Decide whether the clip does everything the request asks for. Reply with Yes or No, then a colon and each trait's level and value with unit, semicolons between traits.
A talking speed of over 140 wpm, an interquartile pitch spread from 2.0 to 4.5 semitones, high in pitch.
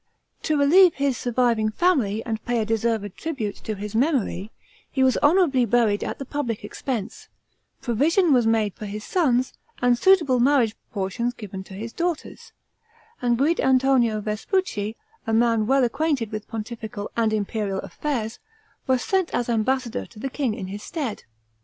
Yes: average, 160 wpm; average, 4.2 semitones; high, 235 Hz